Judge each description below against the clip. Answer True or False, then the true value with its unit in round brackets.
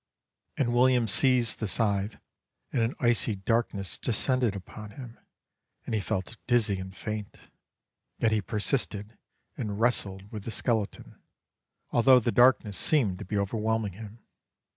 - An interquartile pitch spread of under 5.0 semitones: True (2.9 semitones)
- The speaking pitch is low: True (110 Hz)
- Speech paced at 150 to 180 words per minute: False (140 wpm)